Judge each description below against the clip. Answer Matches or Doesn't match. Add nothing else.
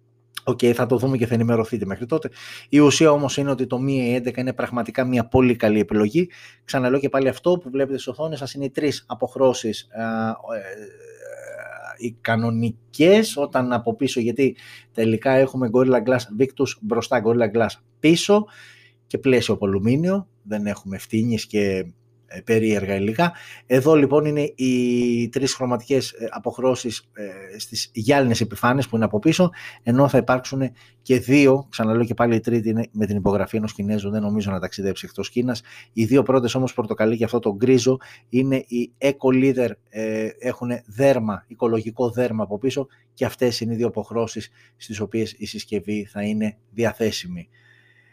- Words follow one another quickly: Doesn't match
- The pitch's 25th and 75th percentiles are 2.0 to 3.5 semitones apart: Matches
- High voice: Doesn't match